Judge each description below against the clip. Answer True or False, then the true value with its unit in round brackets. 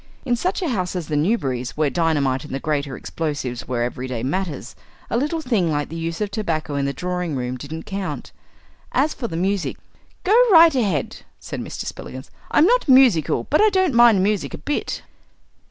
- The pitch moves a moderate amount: False (8.9 semitones)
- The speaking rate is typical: True (190 wpm)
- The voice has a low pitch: False (170 Hz)